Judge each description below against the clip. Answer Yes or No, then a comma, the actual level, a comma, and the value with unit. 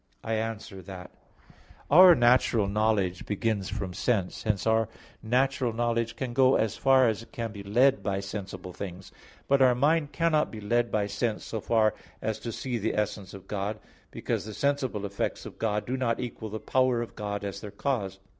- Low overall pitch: Yes, low, 110 Hz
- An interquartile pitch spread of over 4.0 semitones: No, average, 3.4 semitones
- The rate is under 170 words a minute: No, average, 190 wpm